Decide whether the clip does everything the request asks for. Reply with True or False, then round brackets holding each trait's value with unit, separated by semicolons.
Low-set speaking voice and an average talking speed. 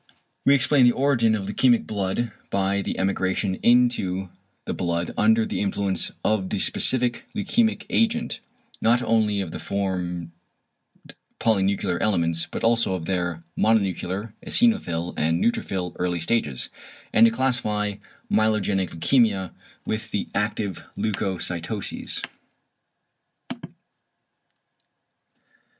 False (100 Hz; 110 wpm)